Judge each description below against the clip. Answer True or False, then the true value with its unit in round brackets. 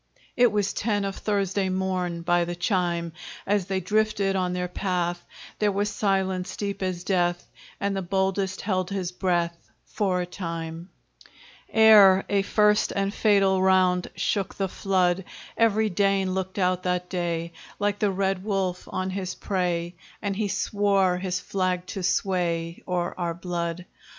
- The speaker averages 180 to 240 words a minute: False (155 wpm)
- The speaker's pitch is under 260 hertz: True (185 Hz)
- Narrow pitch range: True (1.9 semitones)